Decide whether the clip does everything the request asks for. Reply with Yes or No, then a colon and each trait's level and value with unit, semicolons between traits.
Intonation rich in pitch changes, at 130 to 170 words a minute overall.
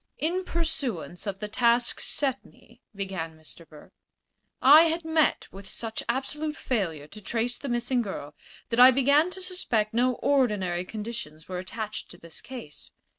Yes: wide, 6.5 semitones; average, 160 wpm